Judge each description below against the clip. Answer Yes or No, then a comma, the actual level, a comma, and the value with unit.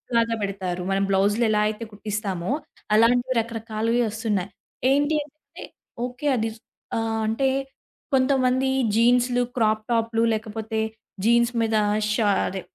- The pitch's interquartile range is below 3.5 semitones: Yes, narrow, 2.4 semitones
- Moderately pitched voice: No, high, 225 Hz